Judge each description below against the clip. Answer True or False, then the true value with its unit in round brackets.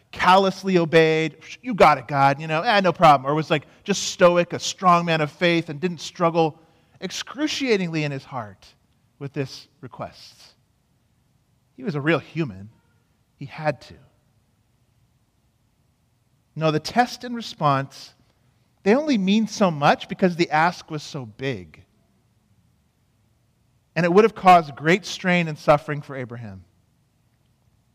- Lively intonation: True (6.3 semitones)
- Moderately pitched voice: True (145 Hz)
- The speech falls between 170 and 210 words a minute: False (140 wpm)